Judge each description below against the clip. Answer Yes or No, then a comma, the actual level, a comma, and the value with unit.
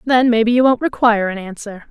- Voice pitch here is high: Yes, high, 225 Hz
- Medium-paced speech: No, fast, 220 wpm